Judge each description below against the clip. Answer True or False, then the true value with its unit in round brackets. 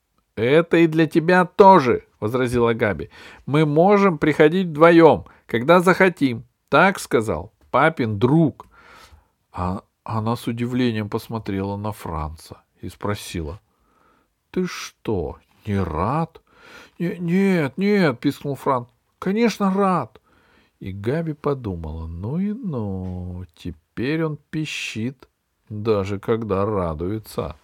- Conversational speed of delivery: False (105 wpm)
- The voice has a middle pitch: False (125 Hz)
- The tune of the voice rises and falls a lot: True (8.6 semitones)